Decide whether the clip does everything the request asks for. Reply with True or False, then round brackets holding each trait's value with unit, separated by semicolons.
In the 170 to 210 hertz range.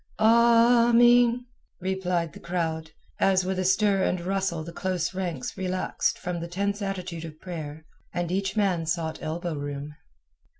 True (185 Hz)